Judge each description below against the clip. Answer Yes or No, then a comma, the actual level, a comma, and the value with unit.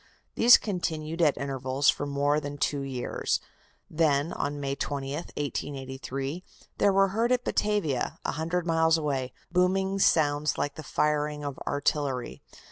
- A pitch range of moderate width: Yes, average, 3.2 semitones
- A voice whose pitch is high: No, medium, 150 Hz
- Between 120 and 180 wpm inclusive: Yes, average, 140 wpm